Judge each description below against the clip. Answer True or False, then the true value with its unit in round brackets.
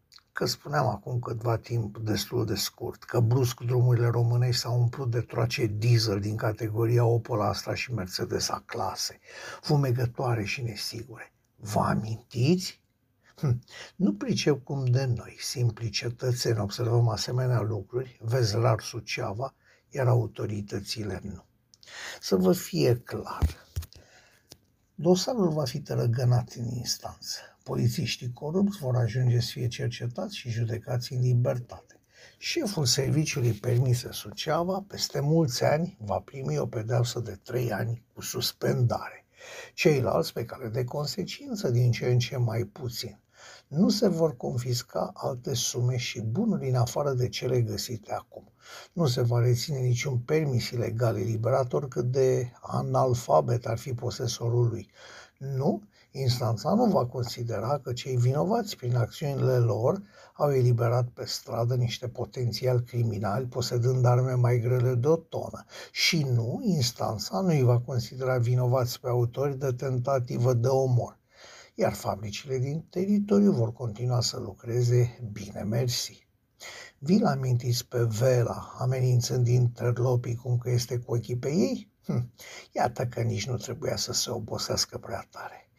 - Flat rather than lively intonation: True (2.0 semitones)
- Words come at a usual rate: True (135 wpm)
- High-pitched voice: False (125 Hz)